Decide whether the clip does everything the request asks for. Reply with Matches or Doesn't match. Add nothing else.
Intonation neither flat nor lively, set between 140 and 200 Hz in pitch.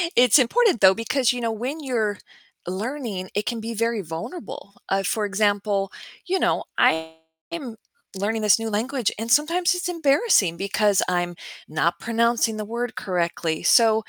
Doesn't match